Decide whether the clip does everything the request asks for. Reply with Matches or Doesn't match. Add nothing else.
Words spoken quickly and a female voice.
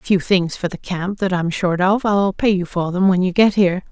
Matches